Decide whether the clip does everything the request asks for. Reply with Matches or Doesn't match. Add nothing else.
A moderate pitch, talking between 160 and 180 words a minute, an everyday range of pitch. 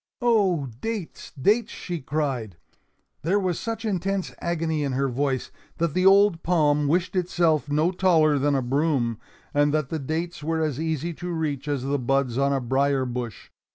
Matches